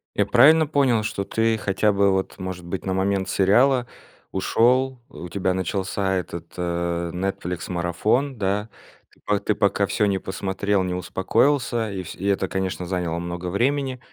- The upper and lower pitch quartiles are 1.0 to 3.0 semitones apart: No, average, 3.6 semitones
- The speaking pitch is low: Yes, very low, 95 Hz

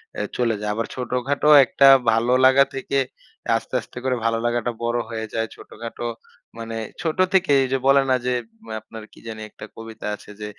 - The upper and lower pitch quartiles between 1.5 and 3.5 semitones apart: Yes, average, 2.7 semitones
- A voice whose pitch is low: Yes, low, 120 Hz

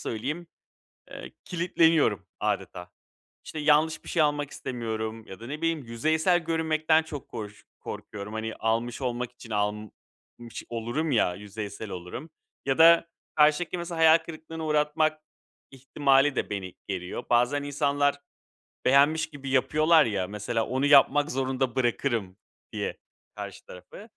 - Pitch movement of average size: No, wide, 5.7 semitones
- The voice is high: No, low, 135 Hz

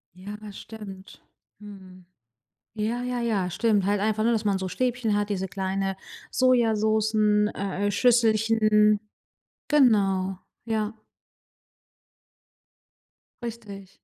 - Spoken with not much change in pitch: Yes, narrow, 2.3 semitones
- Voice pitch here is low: No, high, 210 Hz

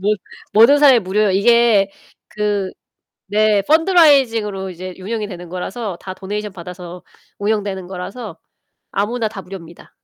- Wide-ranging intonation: No, average, 3.2 semitones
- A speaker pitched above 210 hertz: No, high, 205 Hz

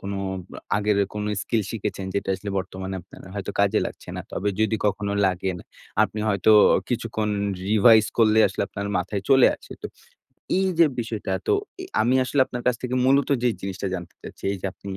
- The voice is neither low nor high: No, low, 105 Hz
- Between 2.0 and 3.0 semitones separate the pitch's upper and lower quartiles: Yes, average, 2.7 semitones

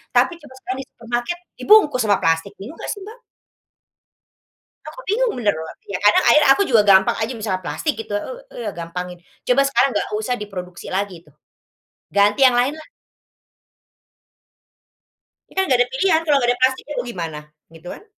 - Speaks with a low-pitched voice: No, high, 240 Hz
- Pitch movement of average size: No, wide, 7.0 semitones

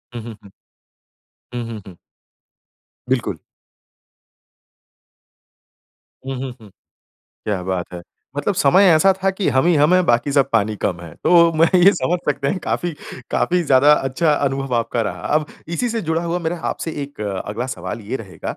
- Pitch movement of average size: No, wide, 7.0 semitones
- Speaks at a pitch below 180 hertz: Yes, low, 135 Hz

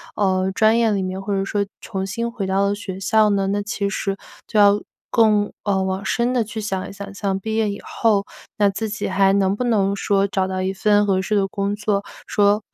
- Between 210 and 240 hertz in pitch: No, high, 200 Hz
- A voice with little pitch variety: Yes, narrow, 1.5 semitones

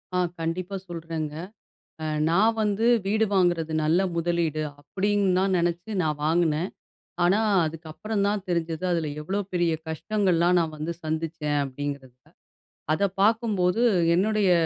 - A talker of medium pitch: Yes, medium, 175 Hz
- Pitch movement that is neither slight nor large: Yes, average, 3.7 semitones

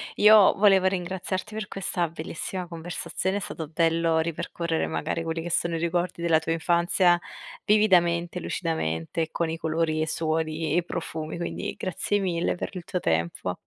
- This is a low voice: No, medium, 170 Hz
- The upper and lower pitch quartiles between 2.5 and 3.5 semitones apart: No, narrow, 2.1 semitones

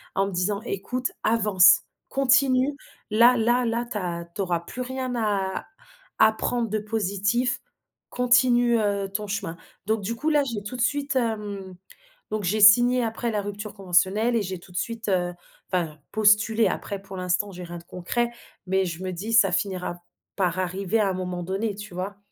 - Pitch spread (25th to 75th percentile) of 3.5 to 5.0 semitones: Yes, average, 3.8 semitones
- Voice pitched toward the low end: No, high, 205 Hz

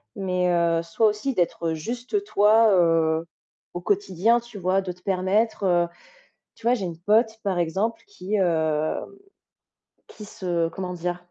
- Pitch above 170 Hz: Yes, medium, 185 Hz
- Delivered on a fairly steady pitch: No, average, 3.9 semitones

